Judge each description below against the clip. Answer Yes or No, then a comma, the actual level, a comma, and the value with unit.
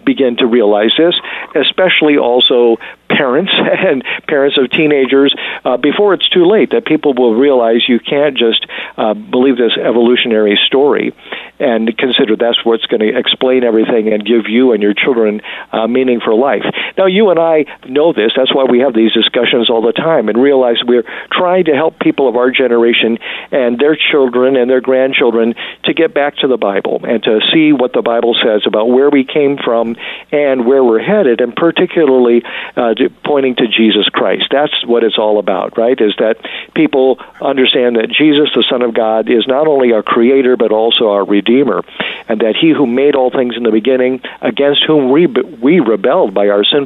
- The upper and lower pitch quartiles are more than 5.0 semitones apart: No, average, 3.8 semitones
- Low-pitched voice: Yes, low, 130 Hz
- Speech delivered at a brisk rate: No, average, 190 wpm